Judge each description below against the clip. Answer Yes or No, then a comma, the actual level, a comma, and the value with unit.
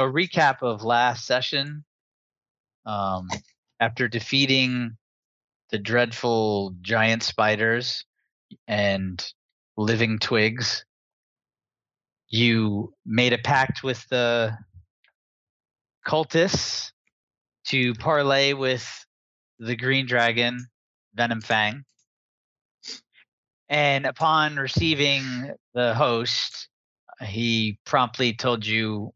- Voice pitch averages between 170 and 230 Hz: No, low, 120 Hz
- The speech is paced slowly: Yes, slow, 80 wpm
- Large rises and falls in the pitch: No, average, 3.0 semitones